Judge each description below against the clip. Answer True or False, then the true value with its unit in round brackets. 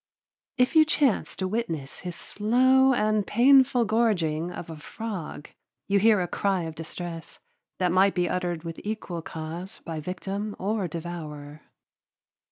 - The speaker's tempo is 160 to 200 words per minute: False (145 wpm)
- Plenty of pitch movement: False (4.8 semitones)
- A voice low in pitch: False (185 Hz)